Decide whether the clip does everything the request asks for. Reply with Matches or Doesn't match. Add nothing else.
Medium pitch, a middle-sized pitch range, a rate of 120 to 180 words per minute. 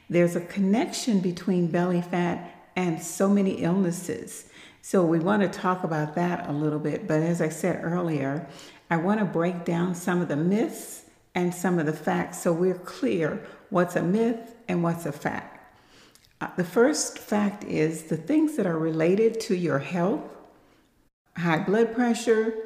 Matches